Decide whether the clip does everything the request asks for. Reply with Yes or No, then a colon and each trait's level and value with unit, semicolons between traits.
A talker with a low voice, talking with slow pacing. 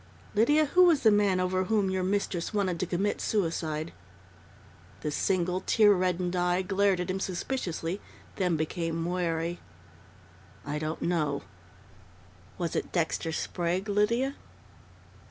No: medium, 185 Hz; slow, 130 wpm